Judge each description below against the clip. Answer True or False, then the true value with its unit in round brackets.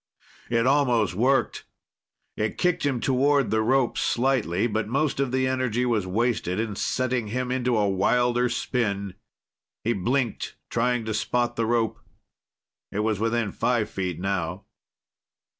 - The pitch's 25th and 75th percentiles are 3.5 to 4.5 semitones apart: False (3.1 semitones)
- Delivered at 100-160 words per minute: True (140 wpm)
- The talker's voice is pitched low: True (120 Hz)